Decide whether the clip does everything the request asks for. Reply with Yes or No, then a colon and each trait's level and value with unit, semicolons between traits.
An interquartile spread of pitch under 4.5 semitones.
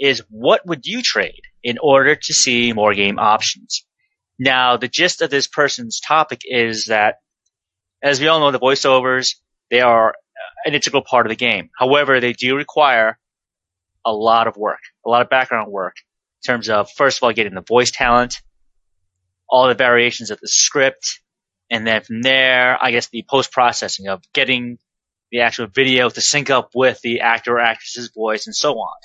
Yes: average, 3.2 semitones